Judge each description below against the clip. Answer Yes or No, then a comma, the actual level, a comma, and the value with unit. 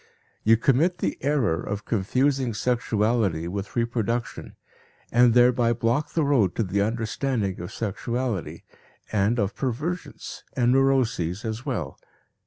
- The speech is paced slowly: Yes, slow, 125 wpm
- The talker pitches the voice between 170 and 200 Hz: No, low, 115 Hz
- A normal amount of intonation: Yes, average, 3.8 semitones